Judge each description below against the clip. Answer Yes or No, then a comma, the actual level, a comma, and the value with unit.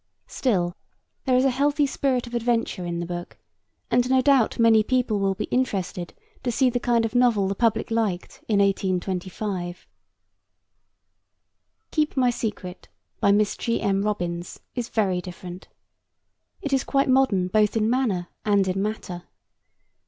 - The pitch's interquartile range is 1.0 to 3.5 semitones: No, average, 4.9 semitones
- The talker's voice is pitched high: Yes, high, 215 Hz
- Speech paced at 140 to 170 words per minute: Yes, average, 150 wpm